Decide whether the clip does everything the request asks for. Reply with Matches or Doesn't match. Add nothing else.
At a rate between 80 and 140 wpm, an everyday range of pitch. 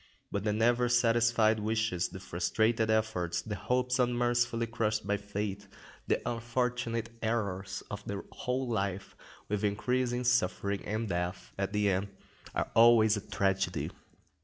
Matches